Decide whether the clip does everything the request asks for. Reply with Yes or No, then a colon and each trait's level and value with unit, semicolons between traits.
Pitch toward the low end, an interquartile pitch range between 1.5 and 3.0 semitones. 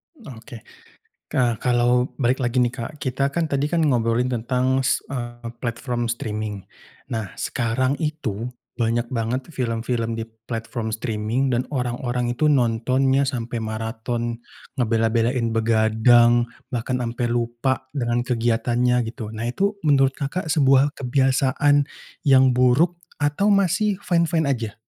Yes: low, 125 Hz; average, 2.7 semitones